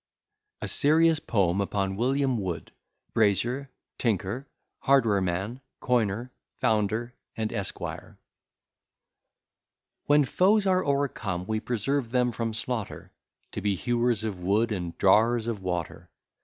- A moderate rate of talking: No, slow, 115 wpm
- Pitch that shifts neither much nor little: Yes, average, 4.3 semitones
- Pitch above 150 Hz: No, low, 115 Hz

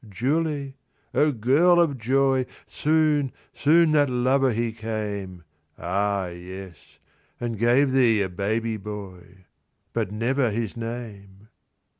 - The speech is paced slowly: Yes, slow, 115 wpm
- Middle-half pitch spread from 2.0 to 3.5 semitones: No, average, 5.1 semitones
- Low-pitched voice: Yes, low, 115 Hz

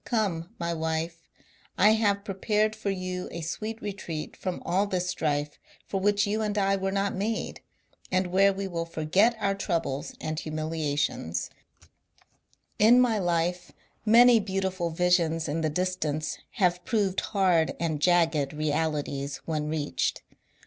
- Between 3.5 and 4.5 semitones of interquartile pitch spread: Yes, average, 3.8 semitones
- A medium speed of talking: Yes, average, 145 wpm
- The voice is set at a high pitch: No, medium, 180 Hz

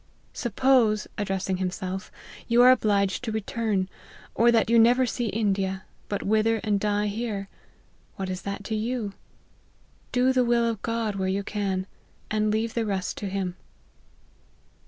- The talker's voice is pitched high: Yes, high, 215 Hz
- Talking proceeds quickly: No, average, 155 wpm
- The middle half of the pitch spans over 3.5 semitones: No, average, 2.9 semitones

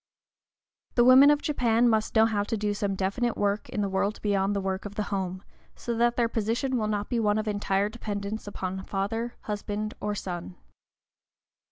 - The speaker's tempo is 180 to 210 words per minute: Yes, average, 190 wpm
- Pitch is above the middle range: Yes, high, 210 Hz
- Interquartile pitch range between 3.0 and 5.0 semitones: No, narrow, 2.4 semitones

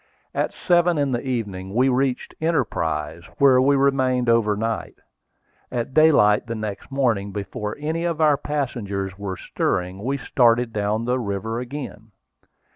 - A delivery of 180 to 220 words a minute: No, average, 140 wpm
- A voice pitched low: Yes, low, 120 Hz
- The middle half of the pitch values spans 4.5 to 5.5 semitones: Yes, average, 4.8 semitones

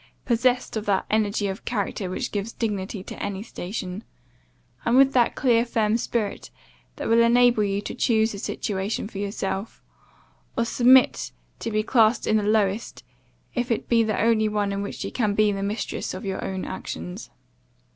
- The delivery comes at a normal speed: Yes, average, 175 wpm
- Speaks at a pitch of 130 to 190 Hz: No, high, 215 Hz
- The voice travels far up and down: No, narrow, 2.6 semitones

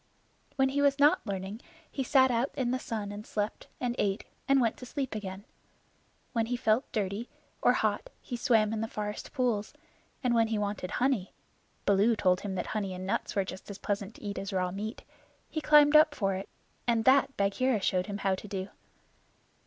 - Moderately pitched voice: No, high, 215 Hz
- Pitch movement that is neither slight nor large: Yes, average, 4.3 semitones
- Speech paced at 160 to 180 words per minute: No, average, 200 wpm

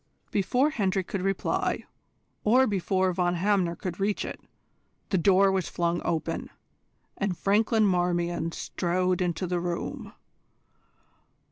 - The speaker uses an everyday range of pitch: No, narrow, 2.2 semitones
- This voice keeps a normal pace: No, slow, 120 wpm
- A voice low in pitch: No, medium, 185 Hz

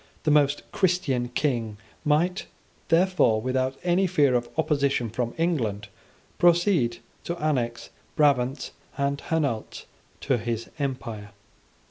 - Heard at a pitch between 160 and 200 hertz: No, medium, 140 Hz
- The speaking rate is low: Yes, slow, 110 wpm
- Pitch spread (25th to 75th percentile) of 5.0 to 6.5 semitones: Yes, average, 5.3 semitones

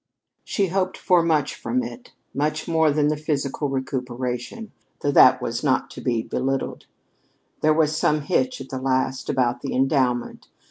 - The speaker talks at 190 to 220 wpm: No, average, 160 wpm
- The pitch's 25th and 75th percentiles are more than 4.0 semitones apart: No, average, 3.6 semitones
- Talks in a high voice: No, medium, 145 Hz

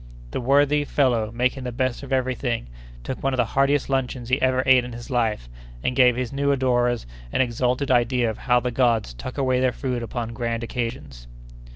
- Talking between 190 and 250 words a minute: Yes, fast, 205 wpm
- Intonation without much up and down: Yes, narrow, 1.8 semitones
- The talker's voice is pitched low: Yes, low, 125 Hz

